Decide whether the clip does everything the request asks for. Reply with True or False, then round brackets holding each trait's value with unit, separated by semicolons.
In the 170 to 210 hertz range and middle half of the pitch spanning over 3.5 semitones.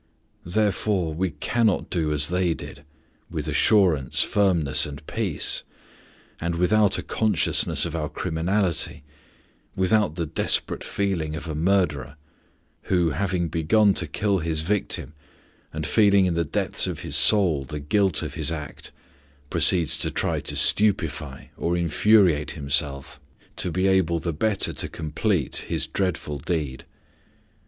False (85 Hz; 4.1 semitones)